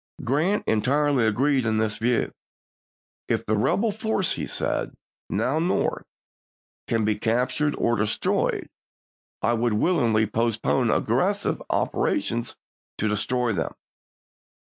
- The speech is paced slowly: Yes, slow, 120 wpm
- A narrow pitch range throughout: No, average, 4.9 semitones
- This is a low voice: Yes, low, 120 Hz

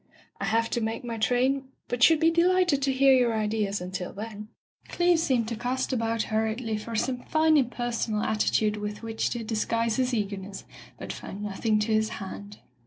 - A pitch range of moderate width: Yes, average, 3.2 semitones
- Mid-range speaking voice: No, high, 230 Hz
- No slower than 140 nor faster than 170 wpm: No, average, 180 wpm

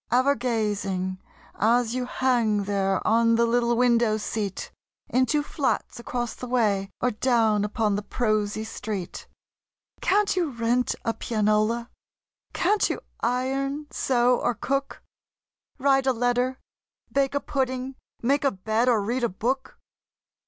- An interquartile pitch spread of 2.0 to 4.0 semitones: Yes, average, 3.2 semitones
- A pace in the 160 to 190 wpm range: No, slow, 135 wpm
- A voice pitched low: No, high, 240 Hz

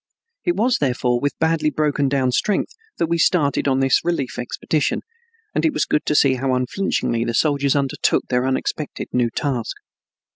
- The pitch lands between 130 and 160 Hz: Yes, medium, 140 Hz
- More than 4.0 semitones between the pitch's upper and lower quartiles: No, average, 3.4 semitones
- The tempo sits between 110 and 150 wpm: No, average, 175 wpm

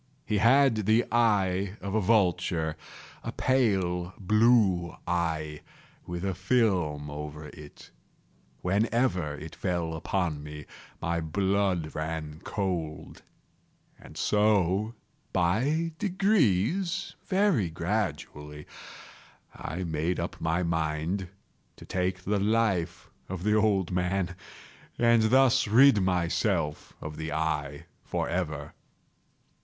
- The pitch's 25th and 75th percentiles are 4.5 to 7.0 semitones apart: Yes, average, 5.1 semitones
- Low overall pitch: Yes, very low, 90 Hz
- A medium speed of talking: No, slow, 100 wpm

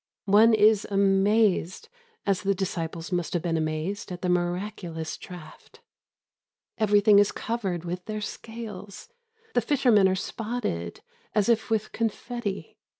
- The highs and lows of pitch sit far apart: No, average, 3.5 semitones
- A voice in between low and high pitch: No, high, 200 Hz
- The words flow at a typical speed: No, slow, 130 wpm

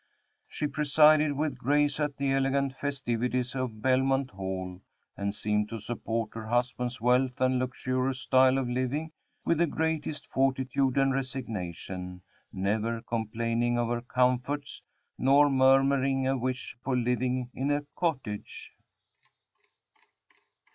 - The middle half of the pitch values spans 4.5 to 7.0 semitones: No, narrow, 2.6 semitones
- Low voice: Yes, low, 130 Hz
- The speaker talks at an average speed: No, slow, 125 wpm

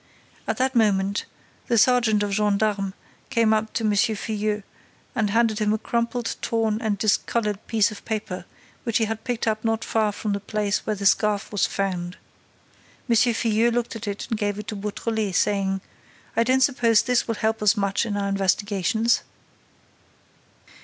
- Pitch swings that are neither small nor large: No, narrow, 2.0 semitones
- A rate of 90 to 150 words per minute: No, average, 175 wpm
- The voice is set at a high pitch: Yes, high, 215 Hz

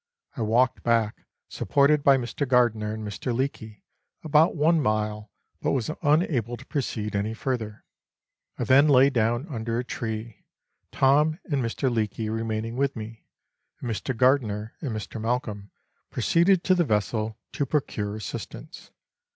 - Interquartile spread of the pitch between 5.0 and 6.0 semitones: No, average, 4.3 semitones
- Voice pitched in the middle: No, low, 120 Hz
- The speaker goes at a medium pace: Yes, average, 145 wpm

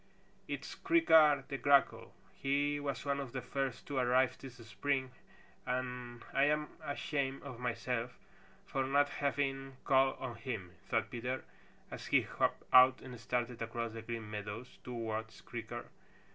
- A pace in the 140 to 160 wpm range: Yes, average, 145 wpm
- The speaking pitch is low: Yes, low, 130 Hz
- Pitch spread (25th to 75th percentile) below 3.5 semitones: Yes, average, 2.8 semitones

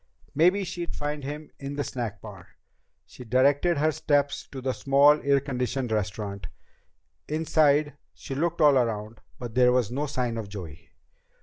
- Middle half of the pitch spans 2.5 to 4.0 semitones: No, average, 4.4 semitones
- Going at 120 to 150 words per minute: No, average, 160 wpm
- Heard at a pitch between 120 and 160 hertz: Yes, low, 135 Hz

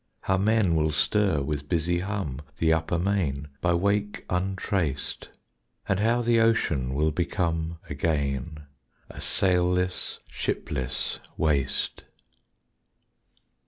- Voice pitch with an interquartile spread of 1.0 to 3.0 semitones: No, average, 4.4 semitones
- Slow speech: Yes, slow, 105 wpm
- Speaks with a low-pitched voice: Yes, very low, 85 Hz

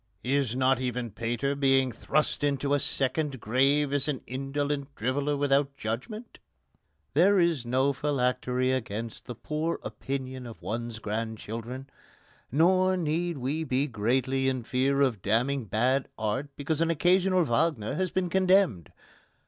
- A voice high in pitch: No, low, 135 Hz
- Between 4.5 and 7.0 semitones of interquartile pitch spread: No, average, 3.3 semitones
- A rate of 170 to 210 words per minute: No, average, 140 wpm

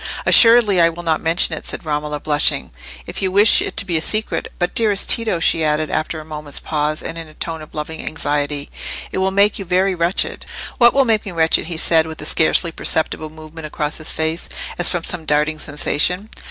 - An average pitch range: Yes, average, 3.2 semitones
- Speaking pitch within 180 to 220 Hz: No, medium, 160 Hz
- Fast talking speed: Yes, fast, 210 wpm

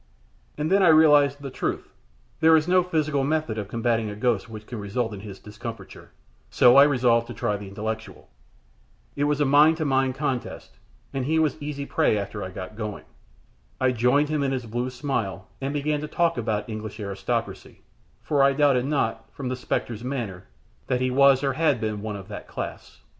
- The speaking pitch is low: Yes, low, 125 Hz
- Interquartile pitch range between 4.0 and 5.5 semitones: Yes, average, 4.9 semitones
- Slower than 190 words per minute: No, average, 200 wpm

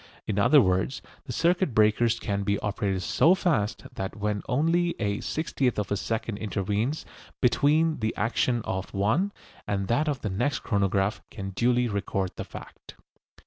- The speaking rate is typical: Yes, average, 165 wpm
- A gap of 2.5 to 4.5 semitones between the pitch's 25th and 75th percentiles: No, average, 5.3 semitones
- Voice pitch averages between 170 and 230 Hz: No, low, 110 Hz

